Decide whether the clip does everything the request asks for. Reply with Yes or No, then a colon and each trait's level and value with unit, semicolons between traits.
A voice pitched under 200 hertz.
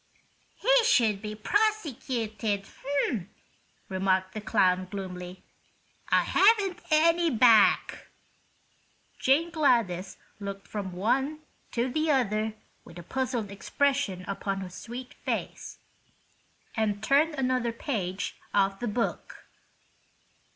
No: high, 225 Hz